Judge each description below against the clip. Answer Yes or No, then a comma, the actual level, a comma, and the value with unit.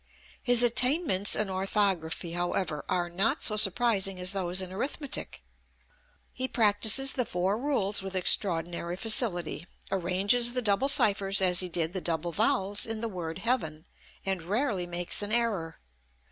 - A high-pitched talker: Yes, high, 195 Hz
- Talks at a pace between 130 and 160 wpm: Yes, average, 145 wpm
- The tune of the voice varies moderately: Yes, average, 4.2 semitones